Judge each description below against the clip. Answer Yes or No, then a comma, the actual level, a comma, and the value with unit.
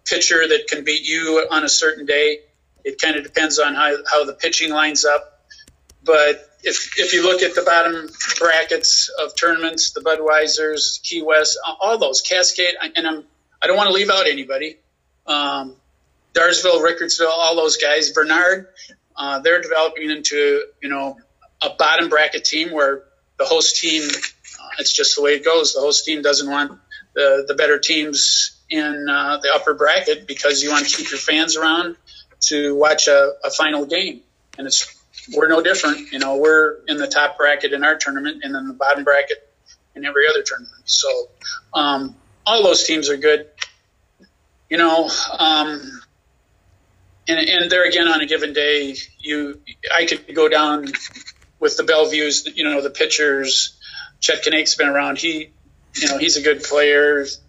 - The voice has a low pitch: No, medium, 155 Hz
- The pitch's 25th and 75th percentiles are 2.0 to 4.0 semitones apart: Yes, average, 3.5 semitones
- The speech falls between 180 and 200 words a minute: No, average, 170 wpm